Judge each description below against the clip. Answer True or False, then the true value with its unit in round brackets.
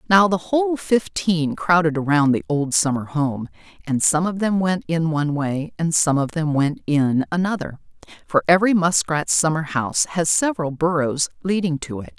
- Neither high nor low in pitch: True (160 Hz)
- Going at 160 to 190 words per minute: True (175 wpm)